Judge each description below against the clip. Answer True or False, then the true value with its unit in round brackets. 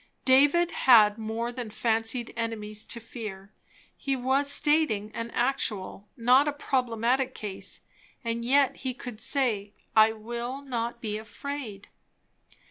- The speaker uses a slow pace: True (125 wpm)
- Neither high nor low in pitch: False (235 Hz)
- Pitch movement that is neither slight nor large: True (3.3 semitones)